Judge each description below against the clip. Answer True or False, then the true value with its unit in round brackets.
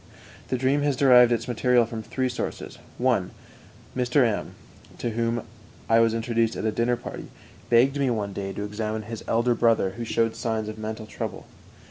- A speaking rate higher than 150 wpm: True (180 wpm)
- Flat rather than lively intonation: True (1.9 semitones)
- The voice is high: False (115 Hz)